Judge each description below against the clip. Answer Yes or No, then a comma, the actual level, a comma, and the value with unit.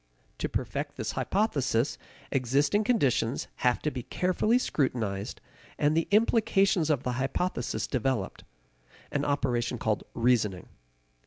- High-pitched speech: No, low, 135 Hz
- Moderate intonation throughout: No, wide, 7.0 semitones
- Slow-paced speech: Yes, slow, 115 wpm